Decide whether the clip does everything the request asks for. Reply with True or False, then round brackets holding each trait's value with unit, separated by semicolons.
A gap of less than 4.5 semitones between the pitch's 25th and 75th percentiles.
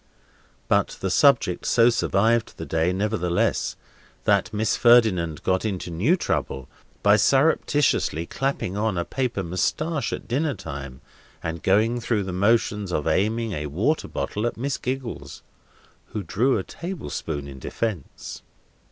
False (5.4 semitones)